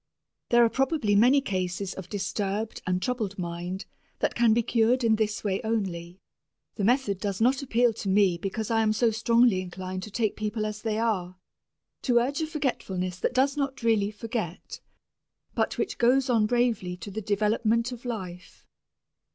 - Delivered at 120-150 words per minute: No, average, 175 wpm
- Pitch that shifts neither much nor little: Yes, average, 3.8 semitones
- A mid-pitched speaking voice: No, high, 215 Hz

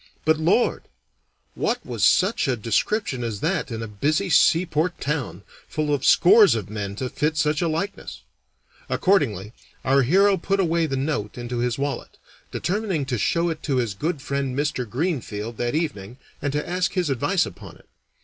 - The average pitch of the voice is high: No, medium, 145 Hz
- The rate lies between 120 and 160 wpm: No, average, 175 wpm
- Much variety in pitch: Yes, wide, 6.1 semitones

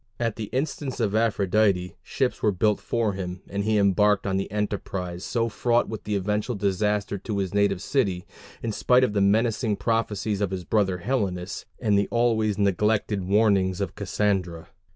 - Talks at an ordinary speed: Yes, average, 170 wpm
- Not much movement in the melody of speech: Yes, narrow, 2.3 semitones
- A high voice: No, low, 105 Hz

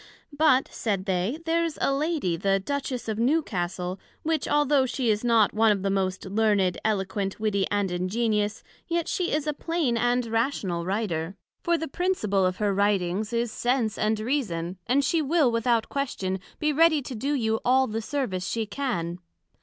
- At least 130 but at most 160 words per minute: No, average, 175 wpm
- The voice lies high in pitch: Yes, high, 225 Hz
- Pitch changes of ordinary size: No, wide, 6.1 semitones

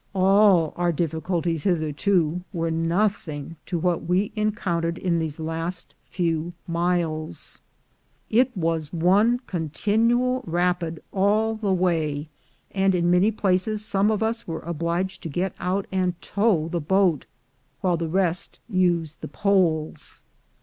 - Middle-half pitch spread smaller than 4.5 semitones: Yes, average, 3.0 semitones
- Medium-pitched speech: Yes, medium, 175 Hz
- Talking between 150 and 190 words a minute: No, slow, 135 wpm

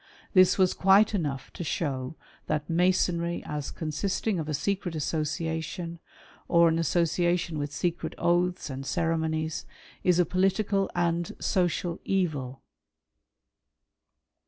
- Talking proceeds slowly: Yes, slow, 120 wpm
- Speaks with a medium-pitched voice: Yes, medium, 170 Hz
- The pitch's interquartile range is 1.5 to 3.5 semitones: Yes, narrow, 2.4 semitones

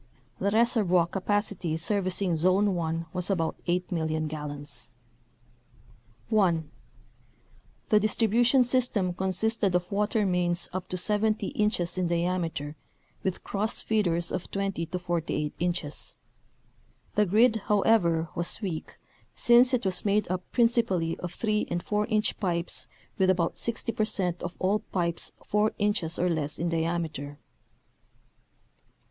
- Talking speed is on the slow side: Yes, slow, 130 wpm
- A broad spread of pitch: No, average, 3.7 semitones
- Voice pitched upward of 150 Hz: Yes, medium, 185 Hz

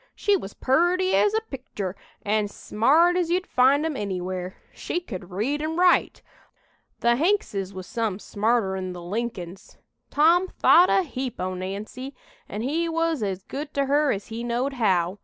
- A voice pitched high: Yes, high, 240 Hz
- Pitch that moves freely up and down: Yes, wide, 8.5 semitones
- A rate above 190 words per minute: No, average, 165 wpm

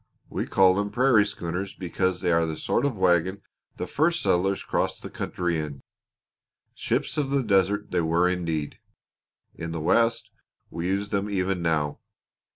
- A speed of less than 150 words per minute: No, average, 160 wpm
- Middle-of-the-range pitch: No, very low, 95 Hz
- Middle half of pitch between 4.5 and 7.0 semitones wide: No, average, 3.4 semitones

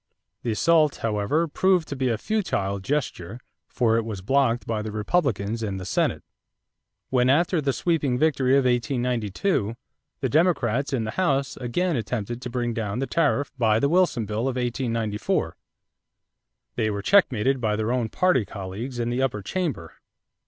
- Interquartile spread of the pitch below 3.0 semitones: No, average, 4.4 semitones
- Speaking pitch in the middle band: No, low, 125 Hz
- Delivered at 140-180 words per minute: Yes, average, 165 wpm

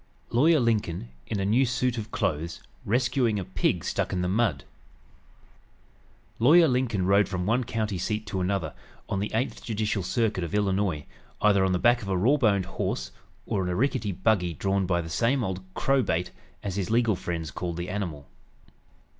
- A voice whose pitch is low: Yes, low, 100 Hz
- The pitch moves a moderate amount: Yes, average, 4.5 semitones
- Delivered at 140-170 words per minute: No, average, 180 wpm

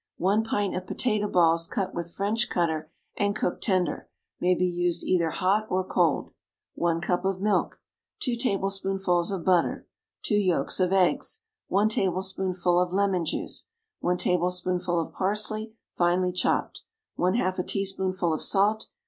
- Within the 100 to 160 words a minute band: Yes, average, 150 wpm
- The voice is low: No, medium, 185 Hz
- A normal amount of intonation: No, narrow, 2.2 semitones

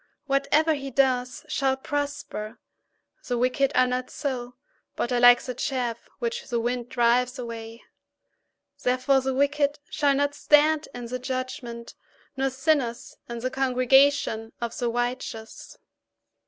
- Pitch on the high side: Yes, very high, 255 Hz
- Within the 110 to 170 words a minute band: Yes, slow, 135 wpm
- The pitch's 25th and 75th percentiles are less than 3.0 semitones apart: Yes, narrow, 2.4 semitones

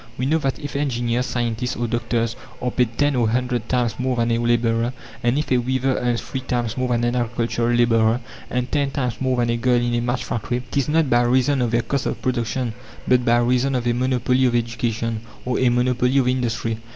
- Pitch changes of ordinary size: No, narrow, 1.4 semitones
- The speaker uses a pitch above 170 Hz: No, low, 120 Hz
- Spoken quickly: Yes, fast, 230 wpm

